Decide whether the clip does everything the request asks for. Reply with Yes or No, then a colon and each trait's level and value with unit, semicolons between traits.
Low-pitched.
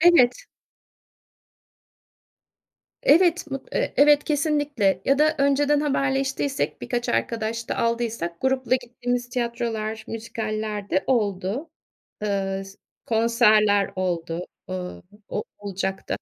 No: high, 235 Hz